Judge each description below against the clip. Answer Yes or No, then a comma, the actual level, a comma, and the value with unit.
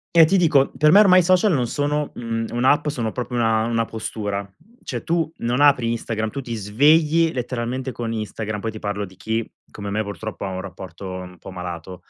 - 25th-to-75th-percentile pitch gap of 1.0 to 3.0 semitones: No, wide, 5.8 semitones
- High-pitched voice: No, low, 115 Hz